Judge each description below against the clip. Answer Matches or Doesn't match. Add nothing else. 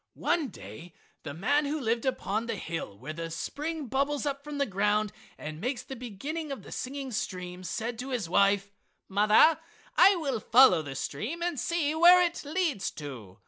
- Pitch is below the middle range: Doesn't match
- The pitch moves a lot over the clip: Matches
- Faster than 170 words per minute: Matches